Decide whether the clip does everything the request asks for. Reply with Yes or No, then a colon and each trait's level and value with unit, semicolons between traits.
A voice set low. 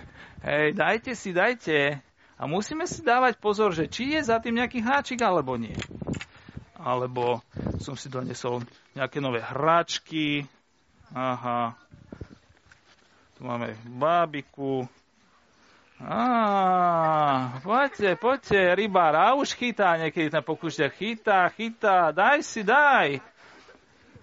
No: medium, 160 Hz